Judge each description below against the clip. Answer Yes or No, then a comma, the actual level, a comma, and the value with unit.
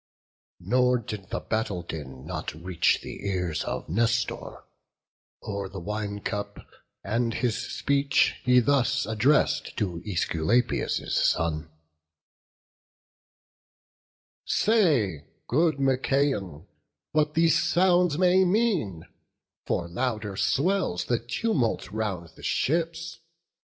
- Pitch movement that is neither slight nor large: No, wide, 7.2 semitones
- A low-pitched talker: Yes, low, 115 Hz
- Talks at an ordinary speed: No, slow, 105 wpm